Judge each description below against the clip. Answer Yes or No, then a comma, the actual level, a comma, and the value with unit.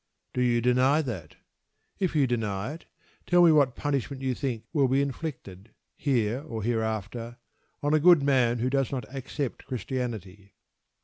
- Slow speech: No, average, 160 wpm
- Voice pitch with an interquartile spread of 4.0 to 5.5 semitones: No, average, 3.6 semitones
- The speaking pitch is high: No, low, 125 Hz